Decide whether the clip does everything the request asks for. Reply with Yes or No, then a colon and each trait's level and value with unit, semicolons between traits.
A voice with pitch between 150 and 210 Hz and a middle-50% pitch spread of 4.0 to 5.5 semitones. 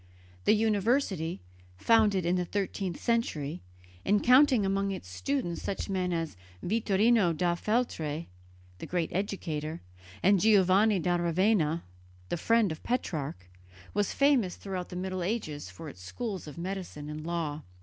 Yes: medium, 185 Hz; average, 4.4 semitones